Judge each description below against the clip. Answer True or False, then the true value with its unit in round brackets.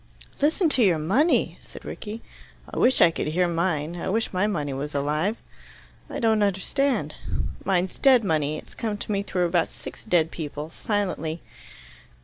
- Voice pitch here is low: False (180 Hz)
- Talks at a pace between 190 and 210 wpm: False (165 wpm)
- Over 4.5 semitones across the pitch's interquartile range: True (5.5 semitones)